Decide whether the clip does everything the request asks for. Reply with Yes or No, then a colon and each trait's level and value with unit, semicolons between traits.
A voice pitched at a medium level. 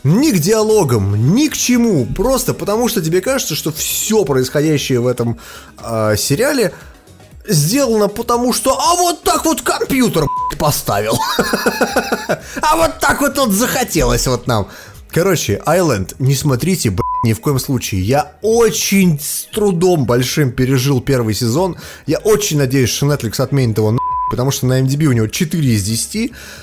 Yes: medium, 155 Hz